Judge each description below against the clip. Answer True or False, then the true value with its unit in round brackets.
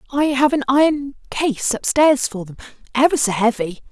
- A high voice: True (260 Hz)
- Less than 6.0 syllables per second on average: True (4.8 syllables/s)